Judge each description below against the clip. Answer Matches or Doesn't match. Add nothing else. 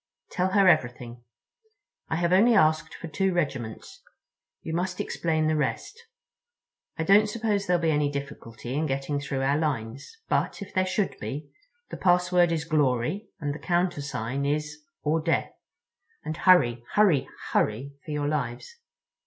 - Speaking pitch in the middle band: Matches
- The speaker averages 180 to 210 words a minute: Doesn't match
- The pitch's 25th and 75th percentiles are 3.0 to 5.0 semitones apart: Matches